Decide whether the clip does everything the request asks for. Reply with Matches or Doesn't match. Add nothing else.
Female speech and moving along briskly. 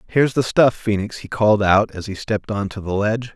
Doesn't match